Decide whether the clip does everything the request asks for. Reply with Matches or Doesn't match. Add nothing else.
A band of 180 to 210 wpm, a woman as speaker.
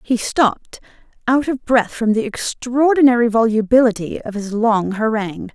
Doesn't match